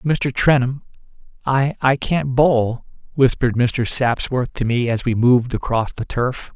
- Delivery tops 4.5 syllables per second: No, 4.2 syllables/s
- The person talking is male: Yes, male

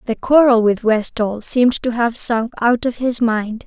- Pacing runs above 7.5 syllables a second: No, 4.4 syllables/s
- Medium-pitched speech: No, high, 235 Hz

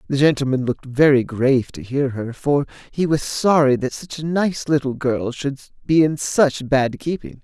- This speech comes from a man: Yes, male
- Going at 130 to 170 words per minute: No, average, 195 wpm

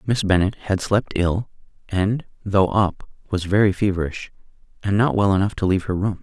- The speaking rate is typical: Yes, average, 185 wpm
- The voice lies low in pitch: Yes, low, 100 Hz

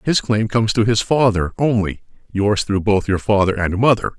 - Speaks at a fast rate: No, average, 185 wpm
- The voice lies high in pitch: No, low, 105 Hz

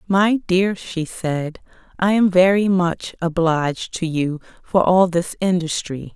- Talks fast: No, average, 145 wpm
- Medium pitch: Yes, medium, 175 Hz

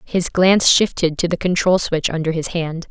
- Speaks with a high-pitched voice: No, medium, 170 Hz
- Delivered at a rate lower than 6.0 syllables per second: Yes, 5.1 syllables/s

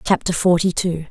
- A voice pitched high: No, medium, 170 Hz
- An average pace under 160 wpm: No, average, 165 wpm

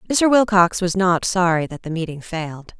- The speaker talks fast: No, average, 195 wpm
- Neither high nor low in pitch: Yes, medium, 180 Hz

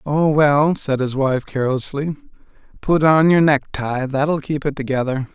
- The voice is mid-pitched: Yes, medium, 145 Hz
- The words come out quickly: No, average, 145 wpm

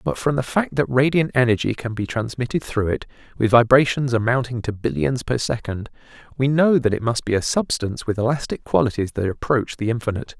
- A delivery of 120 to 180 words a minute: No, average, 195 wpm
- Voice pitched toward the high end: No, low, 120 Hz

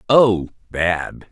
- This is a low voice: Yes, low, 100 Hz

